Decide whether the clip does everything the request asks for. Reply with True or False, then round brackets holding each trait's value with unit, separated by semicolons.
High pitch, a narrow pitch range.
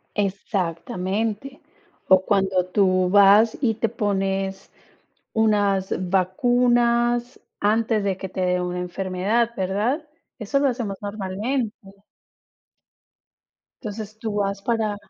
False (205 Hz; 3.1 semitones)